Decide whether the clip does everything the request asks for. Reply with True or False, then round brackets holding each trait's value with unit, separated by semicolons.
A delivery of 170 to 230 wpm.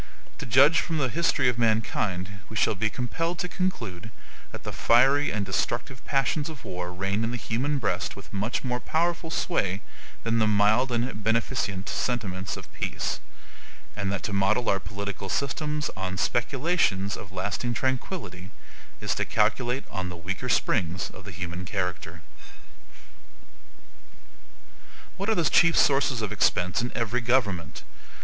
False (155 wpm)